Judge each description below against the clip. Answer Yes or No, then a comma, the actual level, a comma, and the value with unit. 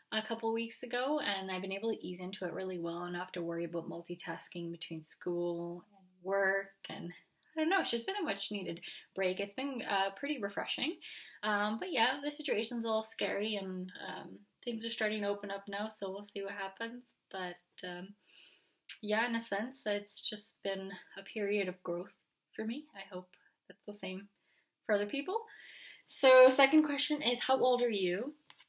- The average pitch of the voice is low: No, high, 205 Hz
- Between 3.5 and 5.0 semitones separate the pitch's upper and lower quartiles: Yes, average, 4.2 semitones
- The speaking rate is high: No, average, 195 wpm